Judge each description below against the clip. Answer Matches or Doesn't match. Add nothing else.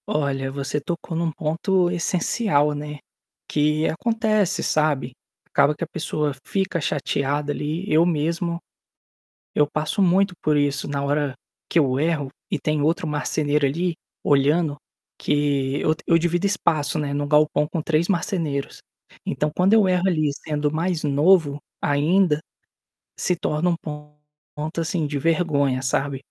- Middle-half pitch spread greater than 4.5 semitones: Doesn't match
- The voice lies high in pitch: Doesn't match